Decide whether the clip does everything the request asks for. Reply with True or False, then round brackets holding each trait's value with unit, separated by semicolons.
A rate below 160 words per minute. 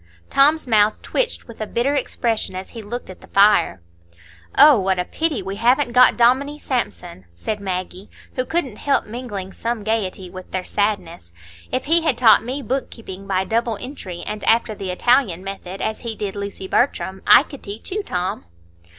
False (185 wpm)